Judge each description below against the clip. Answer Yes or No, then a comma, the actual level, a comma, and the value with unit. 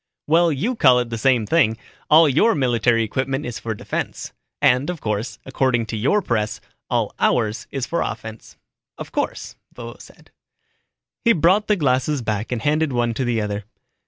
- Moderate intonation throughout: Yes, average, 4.9 semitones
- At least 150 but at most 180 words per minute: Yes, average, 175 wpm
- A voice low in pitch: Yes, low, 125 Hz